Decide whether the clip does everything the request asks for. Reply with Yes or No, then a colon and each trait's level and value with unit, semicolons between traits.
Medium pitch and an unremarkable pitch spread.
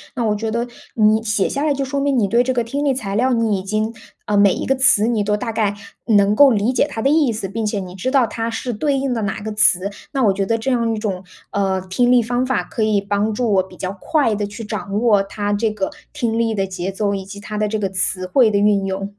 No: high, 215 Hz; average, 3.1 semitones